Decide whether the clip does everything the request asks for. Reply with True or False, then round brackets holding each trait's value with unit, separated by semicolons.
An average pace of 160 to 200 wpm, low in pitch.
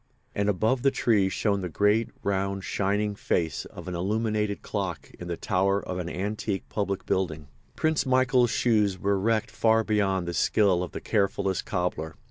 True (170 wpm; 100 Hz)